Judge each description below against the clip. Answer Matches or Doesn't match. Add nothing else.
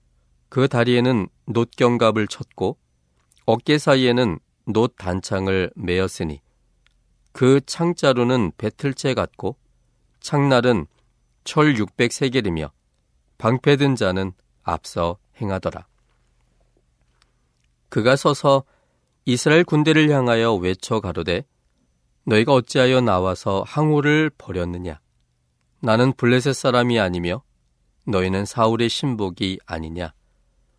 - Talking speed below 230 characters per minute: Matches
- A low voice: Matches